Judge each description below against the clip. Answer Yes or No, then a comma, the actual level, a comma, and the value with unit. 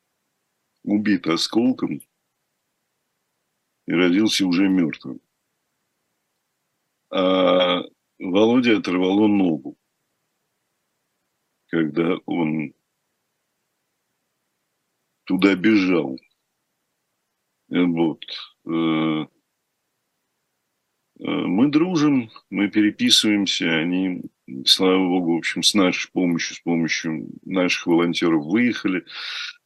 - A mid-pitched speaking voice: No, low, 100 Hz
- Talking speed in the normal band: No, slow, 65 wpm